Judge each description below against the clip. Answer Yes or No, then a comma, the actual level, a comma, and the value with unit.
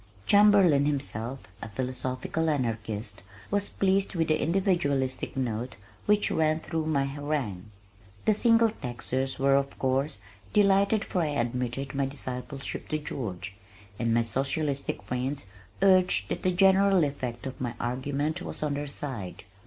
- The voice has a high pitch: No, medium, 140 Hz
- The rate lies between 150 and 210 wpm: No, average, 140 wpm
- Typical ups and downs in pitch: Yes, average, 4.6 semitones